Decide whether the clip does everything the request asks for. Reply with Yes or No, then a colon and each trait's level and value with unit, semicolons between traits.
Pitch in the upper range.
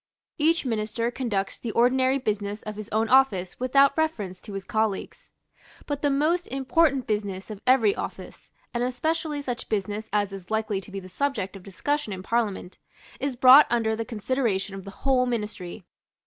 Yes: high, 225 Hz